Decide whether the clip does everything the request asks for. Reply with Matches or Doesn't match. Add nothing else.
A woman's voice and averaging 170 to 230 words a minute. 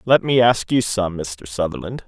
Doesn't match